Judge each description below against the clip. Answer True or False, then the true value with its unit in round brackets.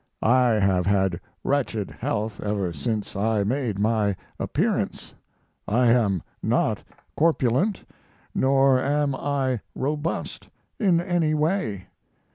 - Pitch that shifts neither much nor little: False (5.8 semitones)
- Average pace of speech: False (105 wpm)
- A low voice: True (120 Hz)